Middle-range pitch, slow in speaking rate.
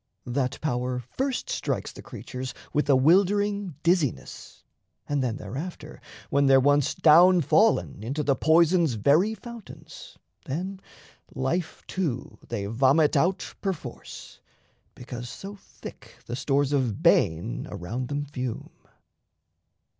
Yes: medium, 145 Hz; slow, 120 wpm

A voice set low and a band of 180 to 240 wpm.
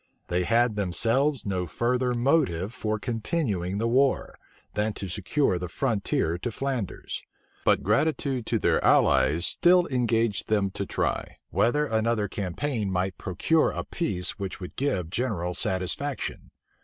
No: low, 110 Hz; average, 145 wpm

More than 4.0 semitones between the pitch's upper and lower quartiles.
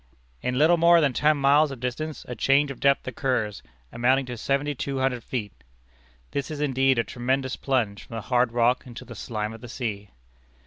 No: average, 2.7 semitones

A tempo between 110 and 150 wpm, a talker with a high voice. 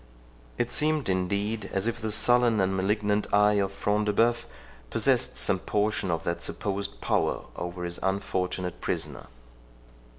No: average, 145 wpm; low, 100 Hz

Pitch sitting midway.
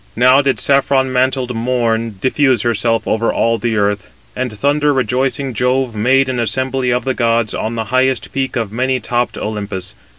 No: low, 125 Hz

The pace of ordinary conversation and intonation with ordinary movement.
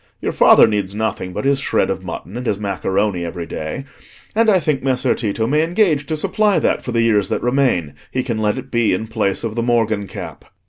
No: fast, 225 wpm; average, 5.0 semitones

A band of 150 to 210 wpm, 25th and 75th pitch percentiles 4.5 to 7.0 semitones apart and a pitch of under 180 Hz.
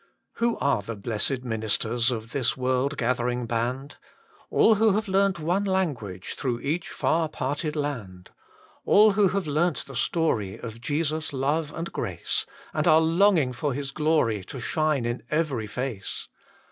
Yes: average, 160 wpm; wide, 5.5 semitones; medium, 140 Hz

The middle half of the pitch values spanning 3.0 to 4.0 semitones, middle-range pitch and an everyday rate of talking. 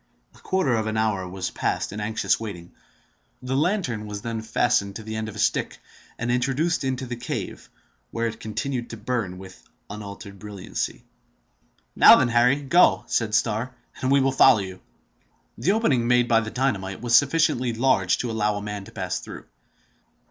No: average, 3.4 semitones; low, 115 Hz; average, 180 wpm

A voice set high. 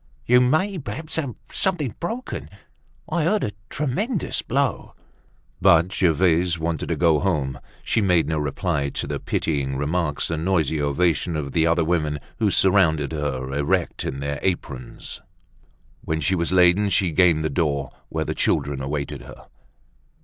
No: very low, 85 Hz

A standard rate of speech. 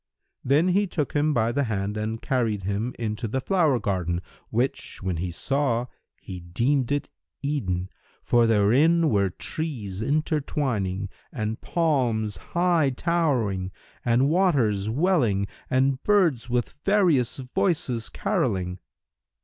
No: slow, 125 wpm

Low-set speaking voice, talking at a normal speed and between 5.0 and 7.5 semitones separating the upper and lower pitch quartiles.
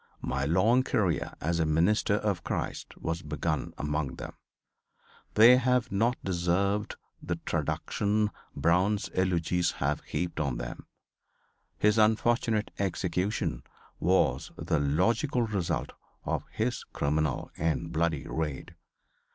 No: very low, 90 Hz; slow, 115 wpm; wide, 5.4 semitones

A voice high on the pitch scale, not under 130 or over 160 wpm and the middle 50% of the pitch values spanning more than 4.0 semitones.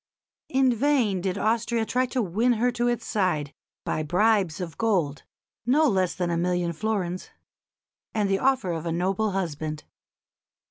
Yes: high, 195 Hz; average, 155 wpm; average, 5.2 semitones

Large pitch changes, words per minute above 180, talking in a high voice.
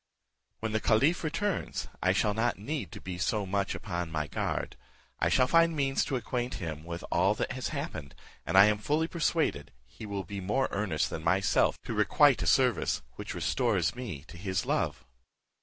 No: wide, 6.7 semitones; average, 190 wpm; low, 105 Hz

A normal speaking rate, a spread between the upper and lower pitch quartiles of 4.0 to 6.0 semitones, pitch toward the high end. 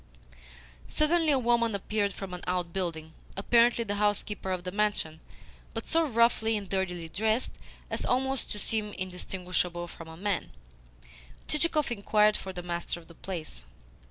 Yes: average, 150 wpm; average, 4.5 semitones; high, 200 Hz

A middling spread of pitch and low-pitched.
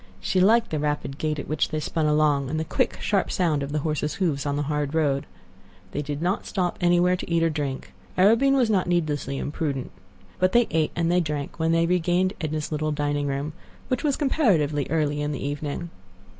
No: average, 3.3 semitones; medium, 155 Hz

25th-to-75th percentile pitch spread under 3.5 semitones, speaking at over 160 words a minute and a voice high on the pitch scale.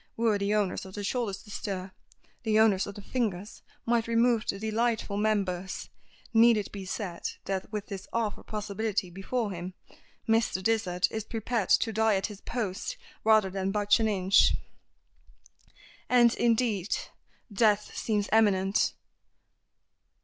No: narrow, 2.5 semitones; average, 140 wpm; high, 210 Hz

